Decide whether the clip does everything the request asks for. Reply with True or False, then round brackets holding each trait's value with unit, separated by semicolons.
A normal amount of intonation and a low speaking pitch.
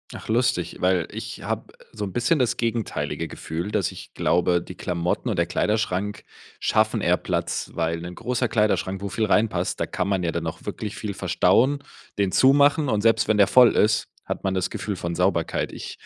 True (4.1 semitones; 100 Hz)